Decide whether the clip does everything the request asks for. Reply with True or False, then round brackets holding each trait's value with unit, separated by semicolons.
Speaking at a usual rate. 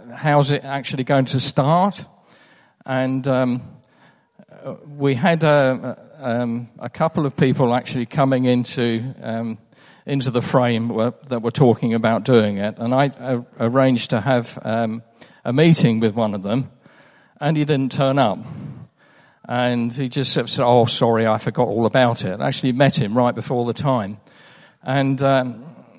True (170 wpm)